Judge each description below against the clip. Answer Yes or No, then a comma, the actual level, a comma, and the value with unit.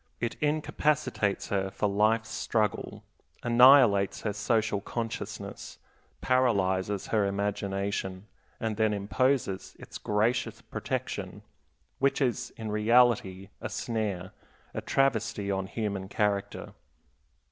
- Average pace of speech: No, slow, 105 wpm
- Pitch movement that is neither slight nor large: Yes, average, 3.1 semitones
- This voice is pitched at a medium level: No, low, 105 Hz